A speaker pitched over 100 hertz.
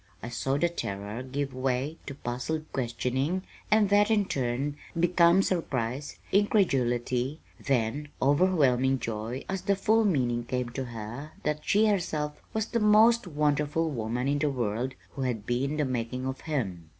Yes: medium, 140 Hz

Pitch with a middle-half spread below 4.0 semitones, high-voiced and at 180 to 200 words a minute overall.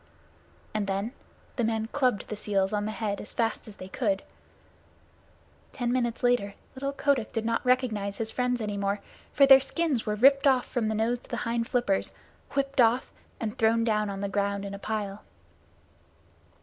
Yes: average, 3.4 semitones; high, 225 Hz; average, 185 wpm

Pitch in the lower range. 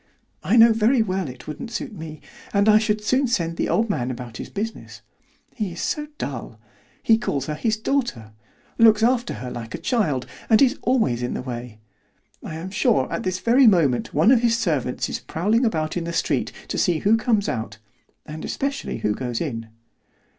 No: high, 190 Hz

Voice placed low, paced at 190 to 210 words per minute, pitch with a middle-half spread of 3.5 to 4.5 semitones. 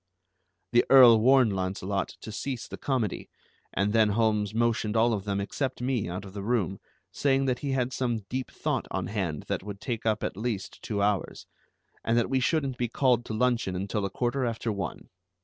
Yes: low, 115 Hz; average, 200 wpm; average, 3.8 semitones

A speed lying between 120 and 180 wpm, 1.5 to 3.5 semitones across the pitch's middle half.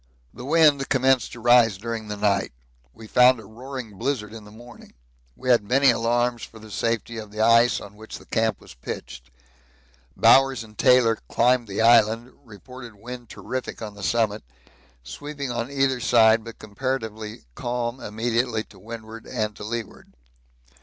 Yes: average, 160 wpm; narrow, 2.5 semitones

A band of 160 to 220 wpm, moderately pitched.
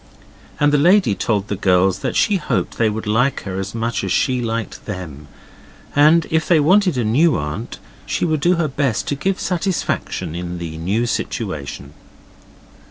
No: average, 175 wpm; low, 115 Hz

